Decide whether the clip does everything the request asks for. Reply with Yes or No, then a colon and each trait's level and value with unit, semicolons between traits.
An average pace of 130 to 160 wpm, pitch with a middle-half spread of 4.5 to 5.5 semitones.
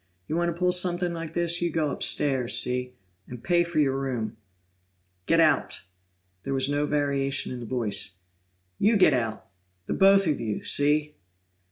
No: average, 170 wpm; average, 5.2 semitones